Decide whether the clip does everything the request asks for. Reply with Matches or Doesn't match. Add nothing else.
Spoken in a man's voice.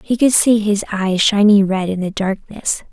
Doesn't match